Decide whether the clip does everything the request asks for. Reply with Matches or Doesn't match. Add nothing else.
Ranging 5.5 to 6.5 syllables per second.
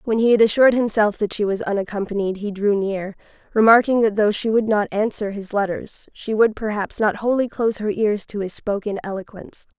Matches